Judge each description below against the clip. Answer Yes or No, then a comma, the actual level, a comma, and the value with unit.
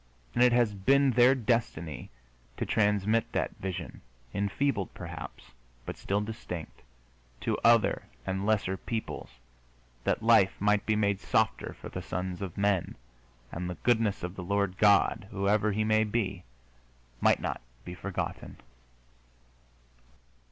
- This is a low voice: Yes, low, 100 Hz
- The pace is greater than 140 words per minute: No, slow, 135 wpm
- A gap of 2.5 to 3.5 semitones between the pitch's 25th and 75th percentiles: Yes, average, 2.8 semitones